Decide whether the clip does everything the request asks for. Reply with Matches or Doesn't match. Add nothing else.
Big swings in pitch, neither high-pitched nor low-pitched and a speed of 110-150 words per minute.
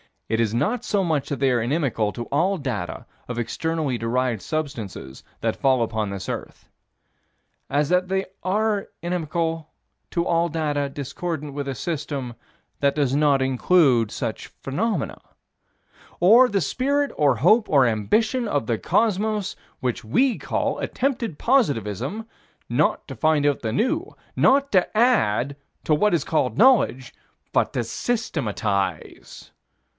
Matches